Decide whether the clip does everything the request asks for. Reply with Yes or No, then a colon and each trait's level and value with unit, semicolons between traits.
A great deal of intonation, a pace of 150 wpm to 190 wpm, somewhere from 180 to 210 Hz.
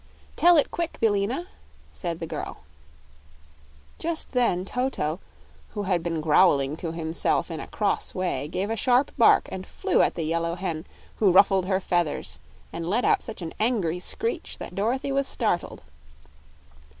Yes: wide, 6.1 semitones; average, 160 wpm; high, 190 Hz